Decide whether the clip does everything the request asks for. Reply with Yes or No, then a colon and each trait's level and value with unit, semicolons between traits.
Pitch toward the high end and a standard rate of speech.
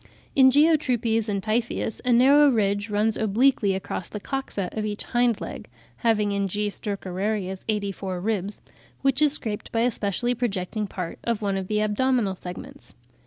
Yes: high, 215 Hz; average, 175 wpm